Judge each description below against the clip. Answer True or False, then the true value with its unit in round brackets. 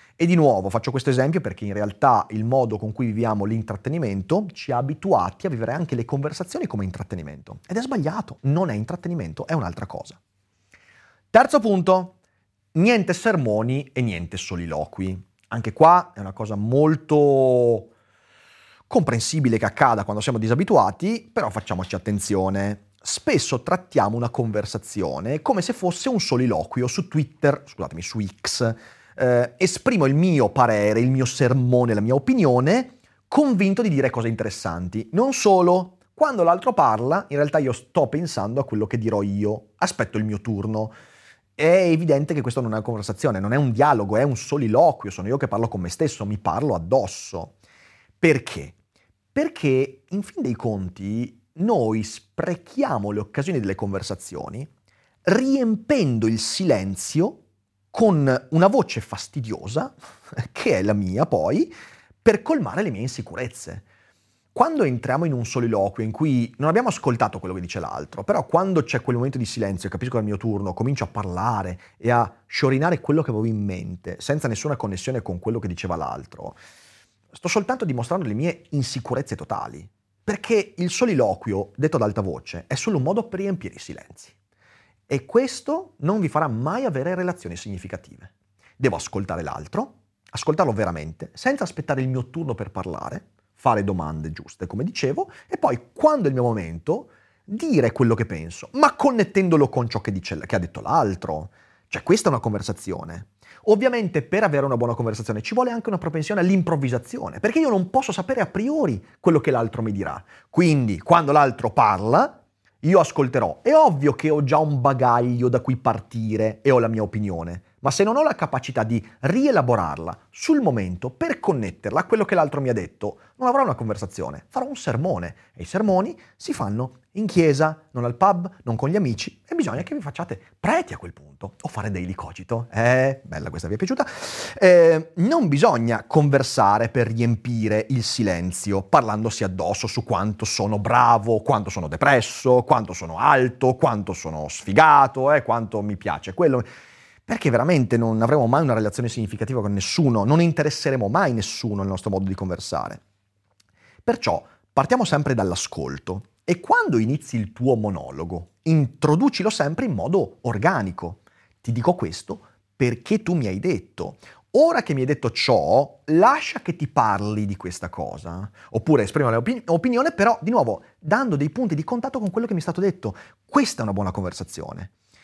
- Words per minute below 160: False (170 wpm)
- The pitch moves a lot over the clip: True (7.6 semitones)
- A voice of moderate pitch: False (120 Hz)